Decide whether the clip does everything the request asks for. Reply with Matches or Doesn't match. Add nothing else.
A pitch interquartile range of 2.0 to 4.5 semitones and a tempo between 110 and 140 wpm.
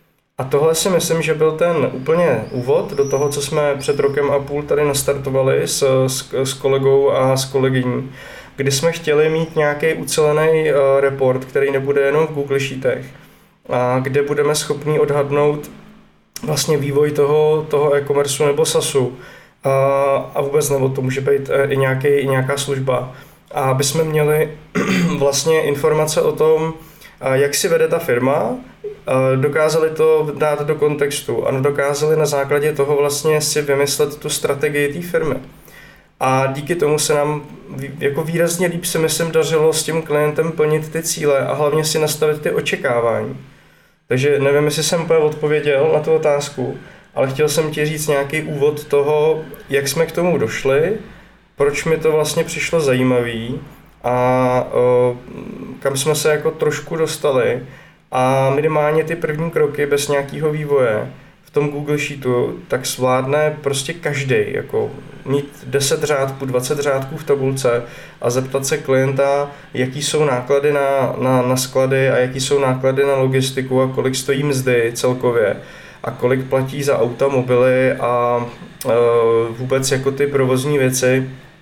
Doesn't match